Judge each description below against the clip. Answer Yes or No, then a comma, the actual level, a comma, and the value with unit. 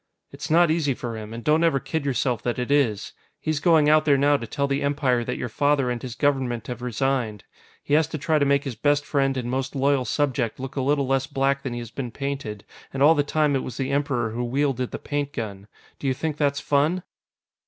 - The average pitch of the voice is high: No, low, 135 Hz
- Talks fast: Yes, fast, 240 wpm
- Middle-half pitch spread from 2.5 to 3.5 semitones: Yes, average, 2.8 semitones